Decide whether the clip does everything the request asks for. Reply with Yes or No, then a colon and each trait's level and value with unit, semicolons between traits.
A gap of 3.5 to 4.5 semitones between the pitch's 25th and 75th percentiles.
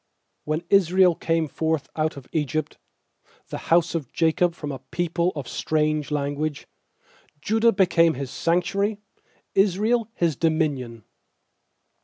No: average, 3.0 semitones